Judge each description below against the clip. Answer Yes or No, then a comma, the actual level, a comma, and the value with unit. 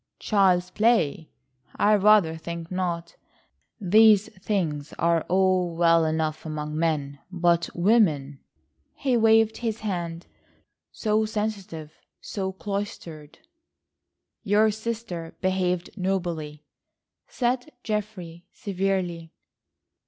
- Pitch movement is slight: No, average, 4.3 semitones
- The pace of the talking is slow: Yes, slow, 95 wpm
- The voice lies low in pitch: No, medium, 185 Hz